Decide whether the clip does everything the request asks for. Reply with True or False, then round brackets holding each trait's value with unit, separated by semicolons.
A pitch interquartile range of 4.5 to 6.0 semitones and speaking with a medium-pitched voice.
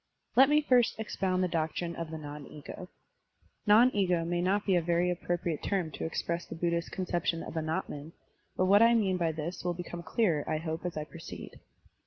False (2.5 semitones; 175 Hz)